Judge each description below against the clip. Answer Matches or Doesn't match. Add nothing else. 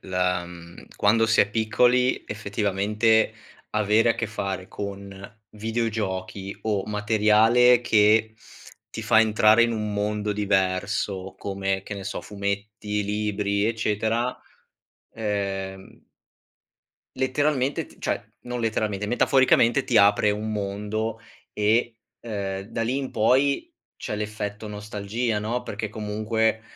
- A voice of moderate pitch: Doesn't match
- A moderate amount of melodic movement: Doesn't match